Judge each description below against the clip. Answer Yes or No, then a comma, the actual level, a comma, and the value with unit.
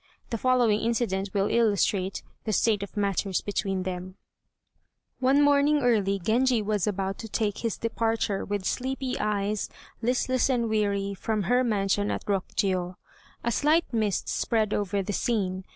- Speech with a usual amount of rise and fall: Yes, average, 3.1 semitones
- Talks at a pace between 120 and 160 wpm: Yes, average, 150 wpm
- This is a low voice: No, high, 210 Hz